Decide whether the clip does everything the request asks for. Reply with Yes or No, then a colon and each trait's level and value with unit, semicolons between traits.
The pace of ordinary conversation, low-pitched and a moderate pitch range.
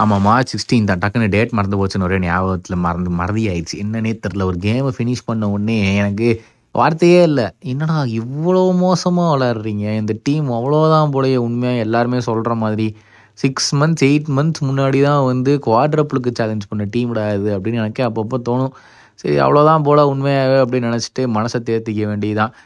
No: fast, 160 wpm; low, 115 Hz; average, 4.2 semitones